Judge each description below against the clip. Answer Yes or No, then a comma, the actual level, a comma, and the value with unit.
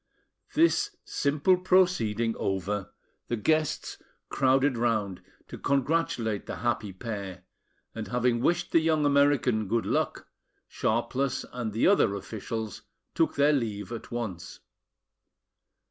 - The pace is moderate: No, slow, 115 wpm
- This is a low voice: Yes, low, 120 Hz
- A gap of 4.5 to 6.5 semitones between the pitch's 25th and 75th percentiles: Yes, average, 5.1 semitones